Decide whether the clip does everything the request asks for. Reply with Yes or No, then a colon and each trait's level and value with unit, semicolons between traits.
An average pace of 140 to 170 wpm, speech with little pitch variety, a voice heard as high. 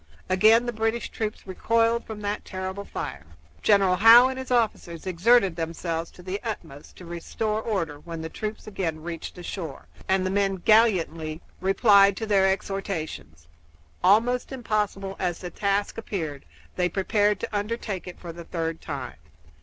No: average, 160 wpm; average, 4.0 semitones; high, 195 Hz